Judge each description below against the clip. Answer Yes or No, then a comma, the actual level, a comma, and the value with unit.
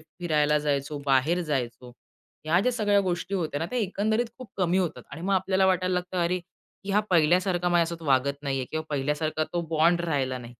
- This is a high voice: No, medium, 170 Hz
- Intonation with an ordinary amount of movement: Yes, average, 3.9 semitones